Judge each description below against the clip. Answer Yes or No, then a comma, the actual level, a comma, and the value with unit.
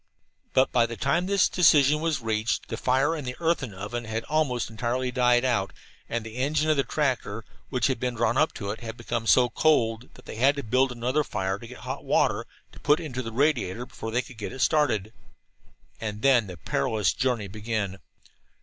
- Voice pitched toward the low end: Yes, low, 120 Hz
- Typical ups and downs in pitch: Yes, average, 3.5 semitones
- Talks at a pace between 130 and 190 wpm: No, fast, 205 wpm